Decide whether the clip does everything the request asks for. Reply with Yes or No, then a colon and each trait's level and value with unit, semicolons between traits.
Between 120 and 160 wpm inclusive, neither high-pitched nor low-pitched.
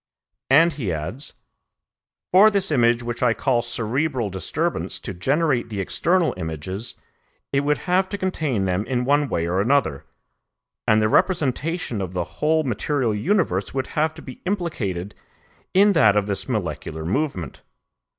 No: average, 150 wpm; low, 125 Hz